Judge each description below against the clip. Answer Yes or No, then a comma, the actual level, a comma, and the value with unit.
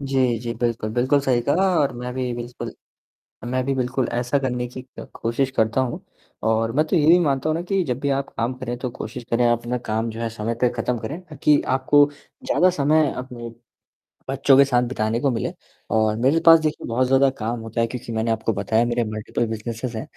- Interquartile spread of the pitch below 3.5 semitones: Yes, average, 2.9 semitones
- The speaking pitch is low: Yes, low, 125 Hz